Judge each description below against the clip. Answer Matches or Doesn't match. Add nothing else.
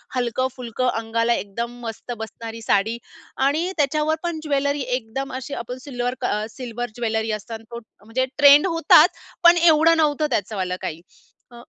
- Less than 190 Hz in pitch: Doesn't match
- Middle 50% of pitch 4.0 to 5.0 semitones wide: Matches